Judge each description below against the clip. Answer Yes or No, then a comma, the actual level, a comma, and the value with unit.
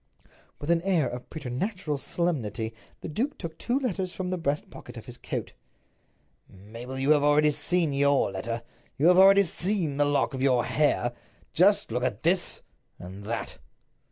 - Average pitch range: No, wide, 6.3 semitones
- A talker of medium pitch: Yes, medium, 145 Hz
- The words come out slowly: No, average, 165 wpm